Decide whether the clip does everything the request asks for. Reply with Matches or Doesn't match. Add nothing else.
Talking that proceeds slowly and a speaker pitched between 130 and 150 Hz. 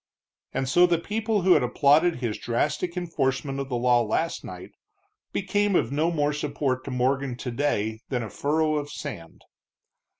Doesn't match